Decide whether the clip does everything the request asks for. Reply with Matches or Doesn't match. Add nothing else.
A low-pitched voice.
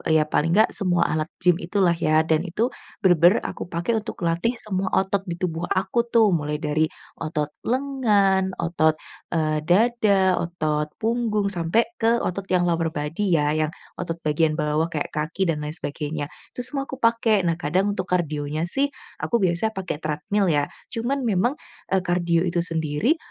Doesn't match